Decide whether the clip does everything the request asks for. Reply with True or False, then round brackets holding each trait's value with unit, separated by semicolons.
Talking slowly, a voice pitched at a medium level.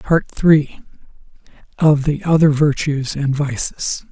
True (115 wpm; 145 Hz)